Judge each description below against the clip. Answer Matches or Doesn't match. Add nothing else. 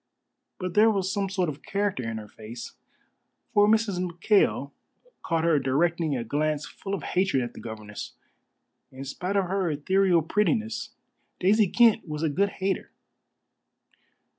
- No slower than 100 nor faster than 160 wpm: Matches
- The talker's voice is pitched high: Doesn't match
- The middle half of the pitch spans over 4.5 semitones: Matches